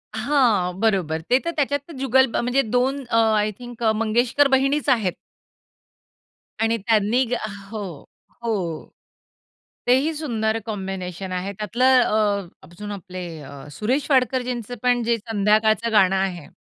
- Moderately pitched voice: No, high, 225 Hz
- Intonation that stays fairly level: No, average, 3.9 semitones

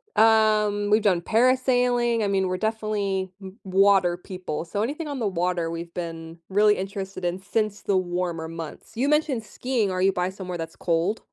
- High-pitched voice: Yes, high, 195 Hz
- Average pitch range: Yes, average, 3.5 semitones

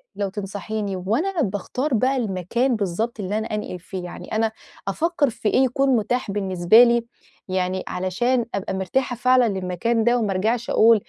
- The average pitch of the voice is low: No, high, 215 Hz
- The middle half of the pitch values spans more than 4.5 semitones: No, average, 4.2 semitones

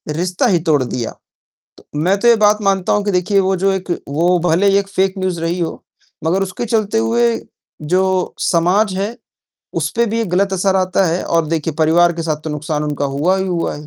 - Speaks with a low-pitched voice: No, medium, 185 Hz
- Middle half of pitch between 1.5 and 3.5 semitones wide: Yes, average, 3.2 semitones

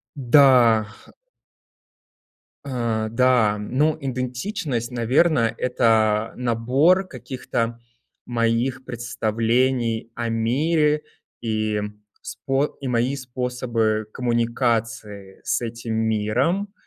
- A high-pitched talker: No, low, 120 Hz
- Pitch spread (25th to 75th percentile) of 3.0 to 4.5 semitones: No, narrow, 2.6 semitones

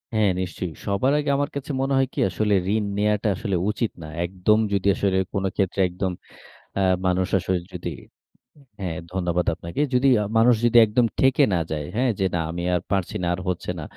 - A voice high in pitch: No, low, 100 Hz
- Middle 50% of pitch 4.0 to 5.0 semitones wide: Yes, average, 4.3 semitones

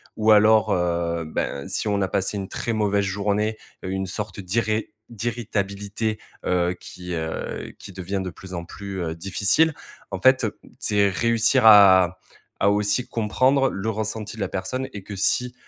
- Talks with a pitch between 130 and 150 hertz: No, low, 100 Hz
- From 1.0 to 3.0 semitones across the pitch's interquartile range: Yes, narrow, 2.6 semitones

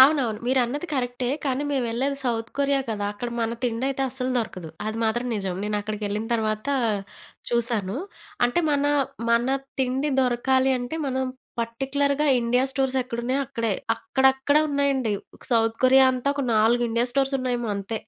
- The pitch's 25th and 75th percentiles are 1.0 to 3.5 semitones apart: Yes, average, 3.0 semitones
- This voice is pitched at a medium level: No, very high, 250 Hz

